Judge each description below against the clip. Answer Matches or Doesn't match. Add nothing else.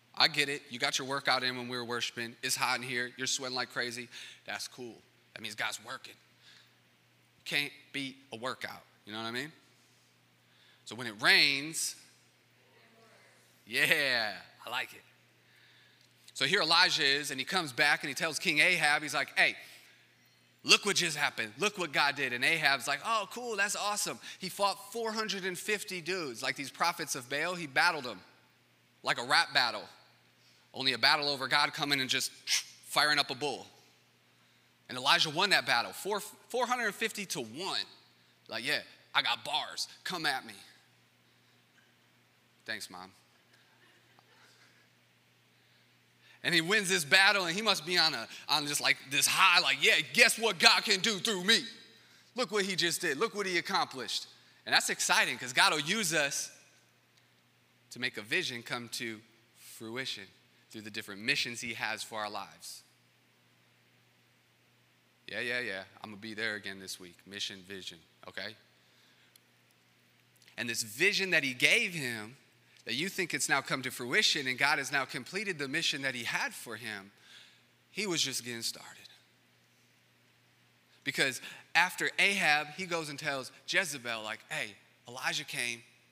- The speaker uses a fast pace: Doesn't match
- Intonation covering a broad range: Matches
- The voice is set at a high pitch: Doesn't match